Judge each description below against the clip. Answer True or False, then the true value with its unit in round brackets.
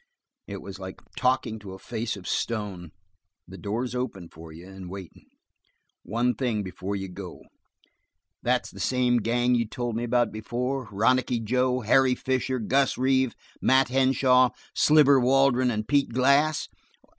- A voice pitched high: False (120 Hz)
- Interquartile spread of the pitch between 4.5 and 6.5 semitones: False (4.0 semitones)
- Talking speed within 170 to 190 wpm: False (150 wpm)